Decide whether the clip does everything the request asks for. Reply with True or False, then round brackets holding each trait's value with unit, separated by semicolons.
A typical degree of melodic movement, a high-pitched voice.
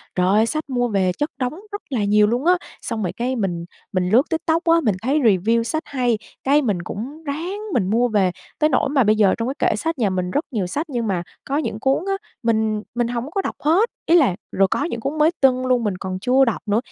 False (5.8 semitones; 240 Hz)